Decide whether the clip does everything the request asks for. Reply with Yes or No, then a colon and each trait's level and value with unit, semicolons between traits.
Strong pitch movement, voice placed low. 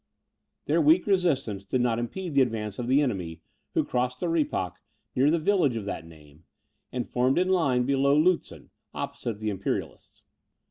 Yes: wide, 6.5 semitones; low, 125 Hz